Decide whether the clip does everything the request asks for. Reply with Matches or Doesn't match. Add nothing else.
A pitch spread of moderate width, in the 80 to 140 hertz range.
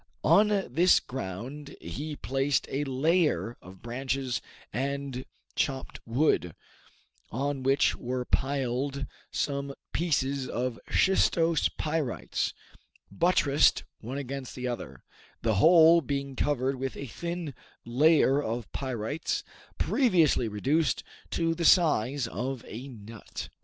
Matches